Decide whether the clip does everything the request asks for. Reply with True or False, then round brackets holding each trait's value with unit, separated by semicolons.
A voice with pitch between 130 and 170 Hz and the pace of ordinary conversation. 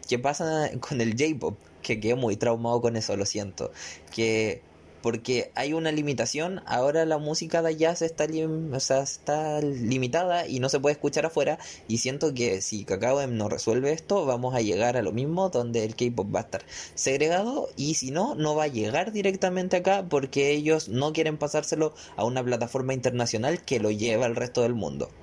False (135 Hz; 195 wpm)